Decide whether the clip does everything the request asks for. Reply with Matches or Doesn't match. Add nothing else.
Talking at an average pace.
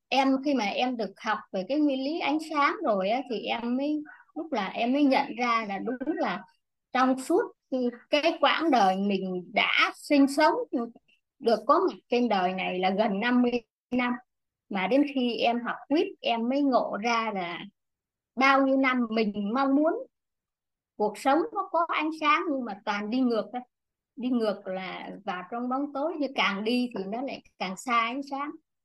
Matches